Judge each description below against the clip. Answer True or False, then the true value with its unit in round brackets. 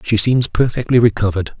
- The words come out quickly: False (150 wpm)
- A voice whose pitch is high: False (115 Hz)